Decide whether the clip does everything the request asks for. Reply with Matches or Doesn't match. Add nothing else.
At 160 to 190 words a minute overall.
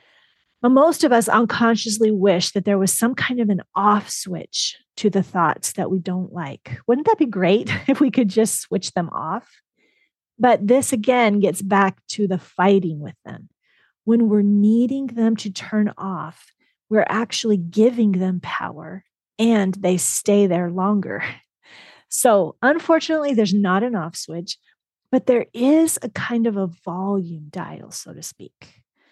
Matches